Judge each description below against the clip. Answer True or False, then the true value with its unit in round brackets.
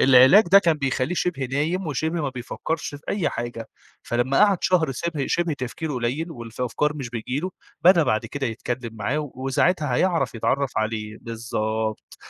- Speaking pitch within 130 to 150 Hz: True (135 Hz)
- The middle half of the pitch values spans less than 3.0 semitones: False (5.3 semitones)